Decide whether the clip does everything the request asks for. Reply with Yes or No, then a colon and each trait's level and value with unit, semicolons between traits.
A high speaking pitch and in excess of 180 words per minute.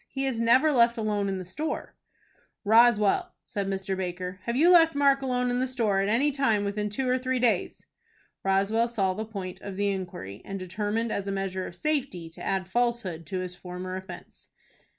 Yes: high, 210 Hz; average, 195 wpm